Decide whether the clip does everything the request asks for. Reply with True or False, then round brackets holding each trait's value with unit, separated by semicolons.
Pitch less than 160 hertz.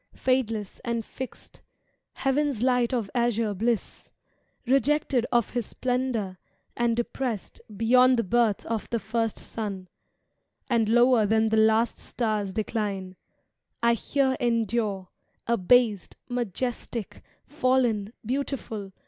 False (230 Hz)